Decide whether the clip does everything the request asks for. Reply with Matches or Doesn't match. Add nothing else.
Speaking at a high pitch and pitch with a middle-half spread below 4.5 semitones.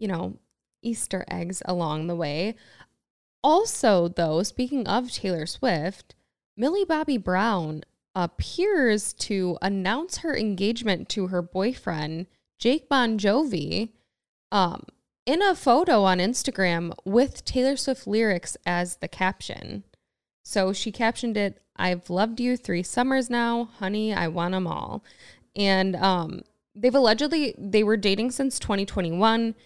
Doesn't match